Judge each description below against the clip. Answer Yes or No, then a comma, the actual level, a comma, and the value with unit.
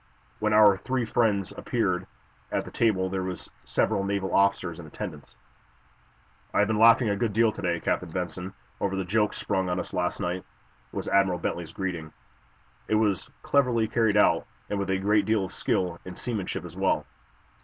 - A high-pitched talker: No, low, 100 Hz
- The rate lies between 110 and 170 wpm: No, average, 180 wpm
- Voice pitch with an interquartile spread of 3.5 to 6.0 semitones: No, average, 2.8 semitones